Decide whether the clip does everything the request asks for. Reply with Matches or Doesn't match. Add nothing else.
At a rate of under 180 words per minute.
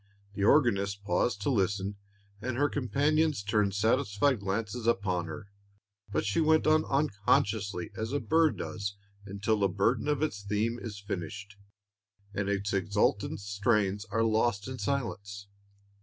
Matches